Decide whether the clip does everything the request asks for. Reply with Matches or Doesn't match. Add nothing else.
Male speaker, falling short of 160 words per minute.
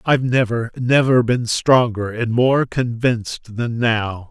Matches